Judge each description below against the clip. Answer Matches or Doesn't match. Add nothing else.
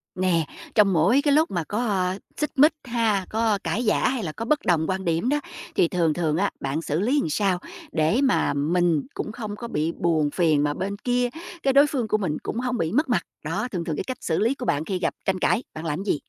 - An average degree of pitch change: Doesn't match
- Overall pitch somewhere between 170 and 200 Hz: Matches